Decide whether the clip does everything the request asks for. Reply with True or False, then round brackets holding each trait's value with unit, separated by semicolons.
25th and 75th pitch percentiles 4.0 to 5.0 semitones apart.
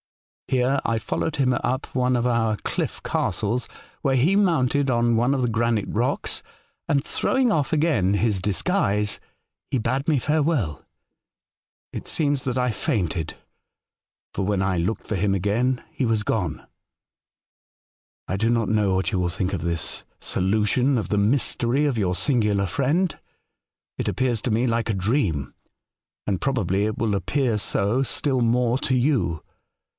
True (4.7 semitones)